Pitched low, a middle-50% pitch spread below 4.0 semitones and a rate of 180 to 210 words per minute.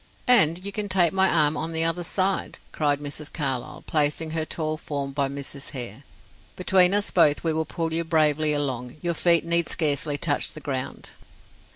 No: medium, 155 Hz; average, 2.9 semitones; average, 185 wpm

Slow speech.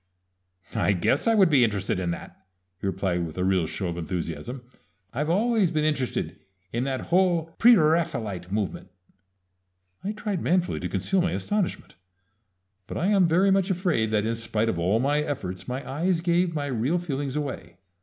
No: average, 175 wpm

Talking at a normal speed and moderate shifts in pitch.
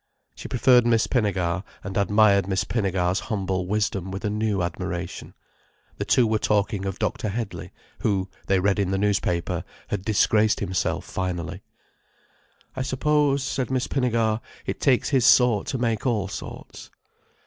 Yes: average, 150 wpm; average, 3.5 semitones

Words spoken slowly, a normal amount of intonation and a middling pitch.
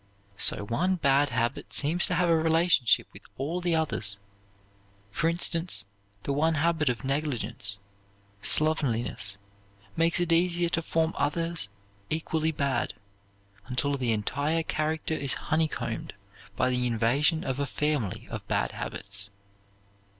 Yes: slow, 130 wpm; average, 4.7 semitones; medium, 150 Hz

